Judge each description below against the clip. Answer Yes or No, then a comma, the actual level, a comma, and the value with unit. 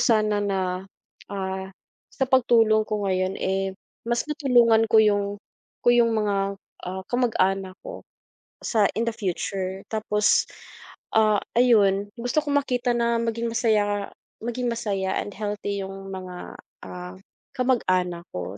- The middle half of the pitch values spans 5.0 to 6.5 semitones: No, average, 3.4 semitones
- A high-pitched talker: Yes, high, 210 Hz